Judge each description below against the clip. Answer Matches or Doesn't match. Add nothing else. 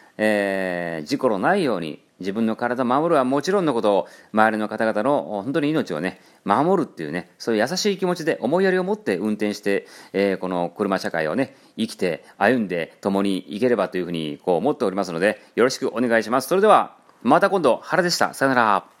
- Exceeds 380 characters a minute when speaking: Matches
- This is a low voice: Matches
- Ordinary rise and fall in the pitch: Doesn't match